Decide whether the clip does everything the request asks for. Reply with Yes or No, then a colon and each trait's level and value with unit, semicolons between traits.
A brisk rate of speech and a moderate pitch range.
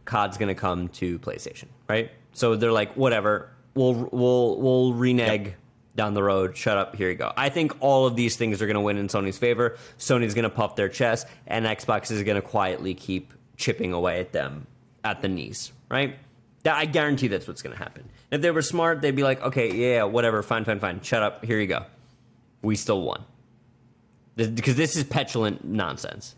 No: average, 195 wpm; average, 3.4 semitones